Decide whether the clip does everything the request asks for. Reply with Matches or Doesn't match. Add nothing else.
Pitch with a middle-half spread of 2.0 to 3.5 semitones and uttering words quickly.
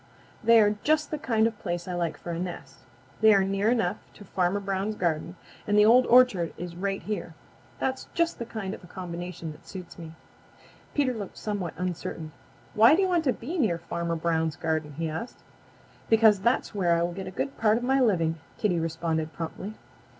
Doesn't match